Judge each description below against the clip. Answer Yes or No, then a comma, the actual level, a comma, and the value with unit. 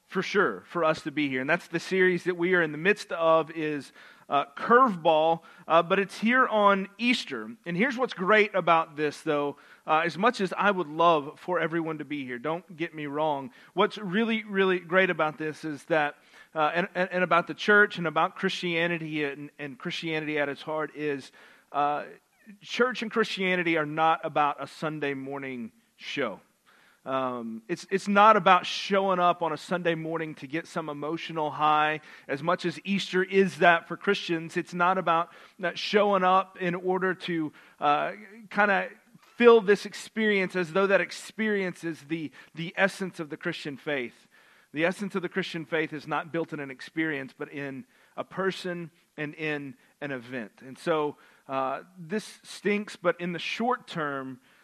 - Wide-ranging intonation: No, average, 3.9 semitones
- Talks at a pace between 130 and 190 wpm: Yes, average, 180 wpm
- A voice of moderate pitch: Yes, medium, 170 Hz